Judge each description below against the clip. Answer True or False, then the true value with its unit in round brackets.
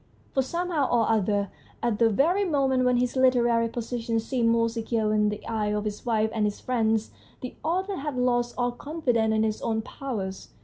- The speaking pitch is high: True (235 Hz)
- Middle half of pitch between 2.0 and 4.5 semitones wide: True (2.9 semitones)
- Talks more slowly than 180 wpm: False (190 wpm)